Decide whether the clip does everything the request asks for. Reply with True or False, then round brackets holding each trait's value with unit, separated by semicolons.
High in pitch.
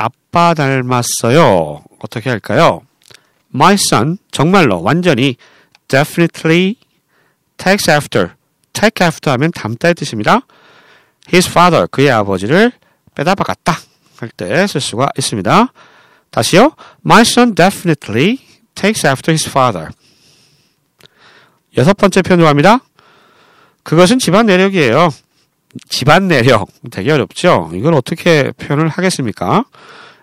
False (165 Hz)